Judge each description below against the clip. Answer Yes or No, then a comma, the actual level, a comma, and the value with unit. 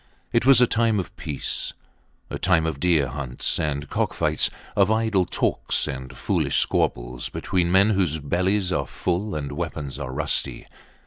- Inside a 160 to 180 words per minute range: Yes, average, 165 wpm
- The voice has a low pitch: Yes, very low, 85 Hz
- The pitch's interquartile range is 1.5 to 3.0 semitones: No, wide, 5.5 semitones